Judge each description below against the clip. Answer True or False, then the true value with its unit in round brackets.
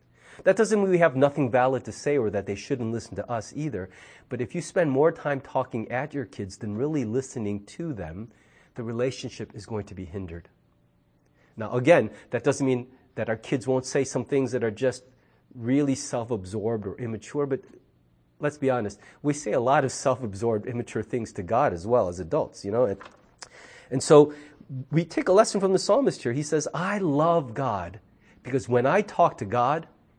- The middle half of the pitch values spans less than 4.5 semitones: False (4.9 semitones)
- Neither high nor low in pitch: False (130 Hz)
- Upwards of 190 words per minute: True (200 wpm)